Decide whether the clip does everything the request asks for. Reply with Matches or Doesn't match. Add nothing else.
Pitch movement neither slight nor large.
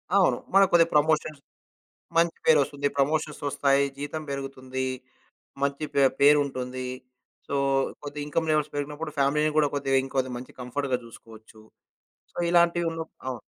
Doesn't match